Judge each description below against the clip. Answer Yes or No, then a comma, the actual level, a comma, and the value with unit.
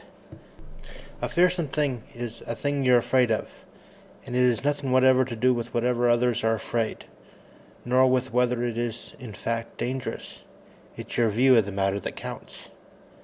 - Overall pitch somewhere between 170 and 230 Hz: No, low, 120 Hz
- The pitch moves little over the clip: Yes, narrow, 1.9 semitones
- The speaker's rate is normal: Yes, average, 170 wpm